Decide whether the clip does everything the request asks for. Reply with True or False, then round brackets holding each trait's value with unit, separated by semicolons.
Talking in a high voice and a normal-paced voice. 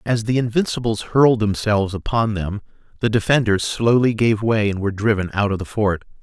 False (110 Hz; 185 wpm)